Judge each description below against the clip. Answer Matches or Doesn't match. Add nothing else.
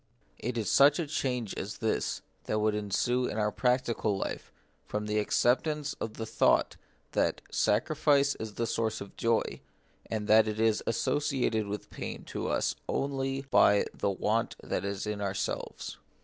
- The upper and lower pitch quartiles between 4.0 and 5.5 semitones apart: Doesn't match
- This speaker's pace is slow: Doesn't match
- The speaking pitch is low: Matches